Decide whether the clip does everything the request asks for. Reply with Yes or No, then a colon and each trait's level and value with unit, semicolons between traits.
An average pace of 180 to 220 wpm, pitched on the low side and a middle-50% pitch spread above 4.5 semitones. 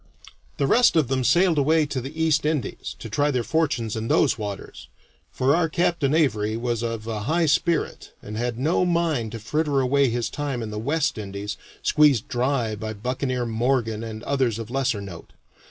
Yes: average, 185 wpm; low, 130 Hz; average, 5.1 semitones